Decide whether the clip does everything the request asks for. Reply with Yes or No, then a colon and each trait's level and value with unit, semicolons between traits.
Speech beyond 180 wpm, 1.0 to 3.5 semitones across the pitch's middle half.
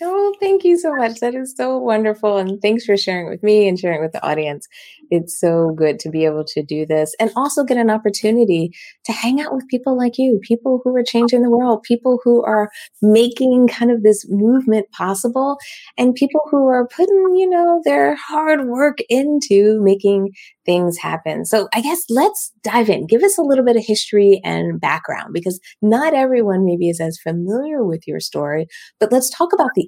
No: average, 200 wpm; average, 5.2 semitones